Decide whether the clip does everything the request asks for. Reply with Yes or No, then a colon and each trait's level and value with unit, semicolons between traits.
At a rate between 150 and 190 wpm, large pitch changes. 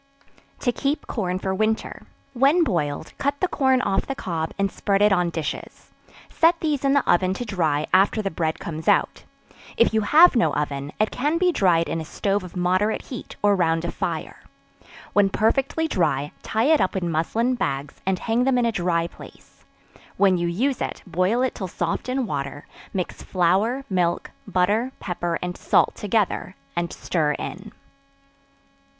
Yes: average, 180 wpm; wide, 6.2 semitones